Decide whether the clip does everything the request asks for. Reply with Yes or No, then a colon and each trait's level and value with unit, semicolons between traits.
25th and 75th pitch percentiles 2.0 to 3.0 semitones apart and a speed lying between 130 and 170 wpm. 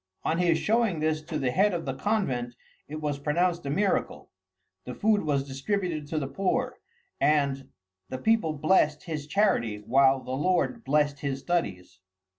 No: average, 5.1 semitones; average, 165 wpm